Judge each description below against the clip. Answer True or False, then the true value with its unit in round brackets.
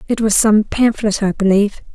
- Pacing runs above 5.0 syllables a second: True (5.4 syllables/s)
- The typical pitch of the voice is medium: False (210 Hz)